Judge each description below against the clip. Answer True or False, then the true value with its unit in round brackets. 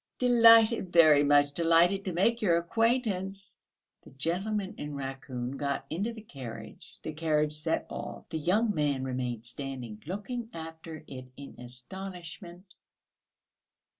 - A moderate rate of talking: False (130 wpm)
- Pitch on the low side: False (165 Hz)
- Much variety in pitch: True (5.7 semitones)